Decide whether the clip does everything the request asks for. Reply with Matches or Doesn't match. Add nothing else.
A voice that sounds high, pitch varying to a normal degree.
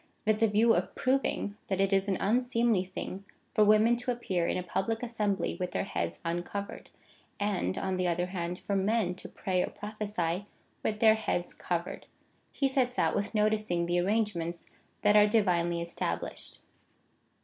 Matches